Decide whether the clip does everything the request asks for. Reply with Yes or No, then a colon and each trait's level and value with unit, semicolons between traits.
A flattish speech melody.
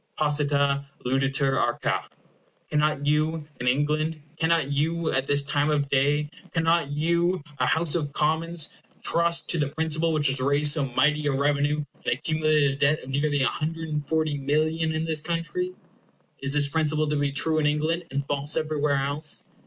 Yes: narrow, 2.0 semitones